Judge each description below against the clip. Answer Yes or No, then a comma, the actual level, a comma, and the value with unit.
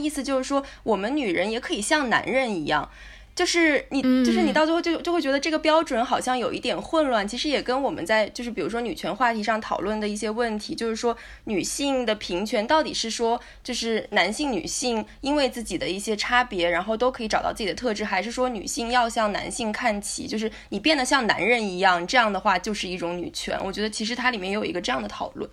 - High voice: Yes, high, 240 Hz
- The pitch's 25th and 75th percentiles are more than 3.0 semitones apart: Yes, average, 4.1 semitones